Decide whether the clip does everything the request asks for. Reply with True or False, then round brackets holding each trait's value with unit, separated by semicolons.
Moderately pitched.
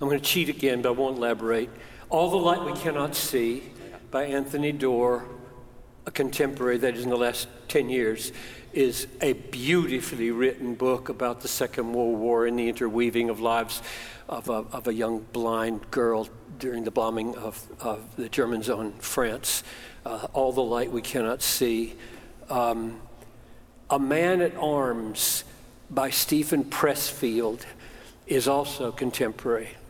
False (125 Hz)